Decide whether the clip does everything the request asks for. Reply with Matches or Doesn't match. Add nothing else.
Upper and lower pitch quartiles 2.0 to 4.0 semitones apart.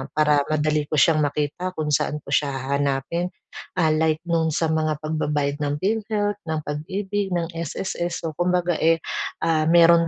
Matches